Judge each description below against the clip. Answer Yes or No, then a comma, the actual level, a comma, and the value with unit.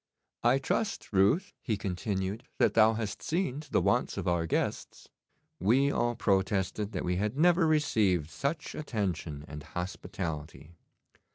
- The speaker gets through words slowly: No, average, 145 wpm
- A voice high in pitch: No, low, 105 Hz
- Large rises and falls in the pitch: Yes, wide, 7.1 semitones